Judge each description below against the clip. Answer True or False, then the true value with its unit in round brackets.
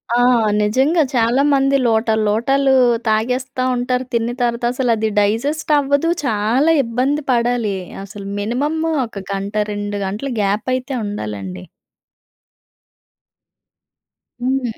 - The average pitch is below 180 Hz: False (240 Hz)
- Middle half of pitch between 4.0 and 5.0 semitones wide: True (4.4 semitones)